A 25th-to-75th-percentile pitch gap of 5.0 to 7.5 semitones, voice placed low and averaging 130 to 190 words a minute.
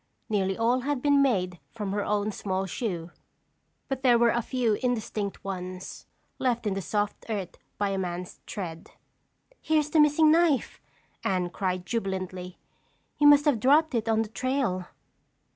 No: wide, 5.4 semitones; high, 215 Hz; average, 160 wpm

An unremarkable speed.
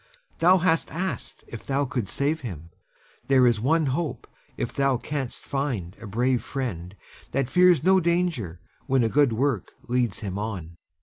Yes: average, 165 wpm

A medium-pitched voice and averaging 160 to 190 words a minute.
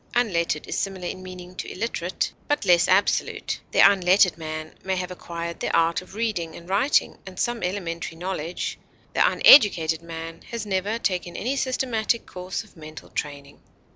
Yes: medium, 180 Hz; average, 165 wpm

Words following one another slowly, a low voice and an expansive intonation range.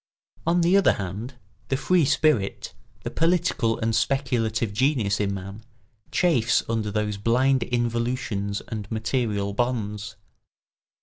No: slow, 120 wpm; low, 115 Hz; average, 4.2 semitones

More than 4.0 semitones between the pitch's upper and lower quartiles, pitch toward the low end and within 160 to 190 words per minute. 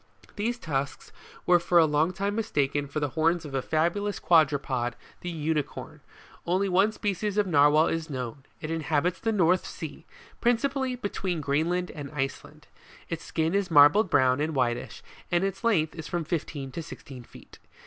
No: average, 4.7 semitones; medium, 165 Hz; average, 170 wpm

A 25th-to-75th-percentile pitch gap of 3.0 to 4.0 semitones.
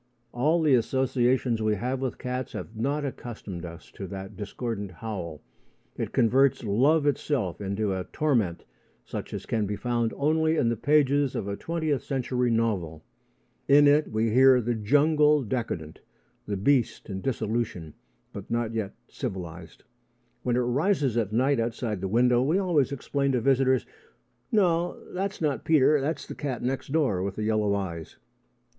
No: average, 5.2 semitones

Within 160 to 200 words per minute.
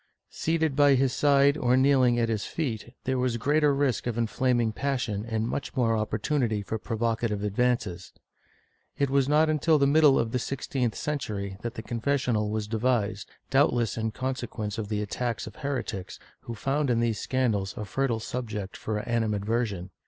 Yes: average, 170 wpm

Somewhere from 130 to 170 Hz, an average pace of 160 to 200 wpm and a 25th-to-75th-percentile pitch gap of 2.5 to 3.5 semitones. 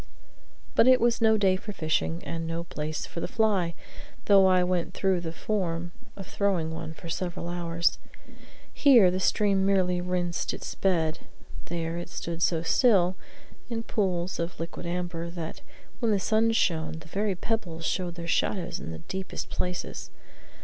No: medium, 180 Hz; average, 165 wpm; average, 2.8 semitones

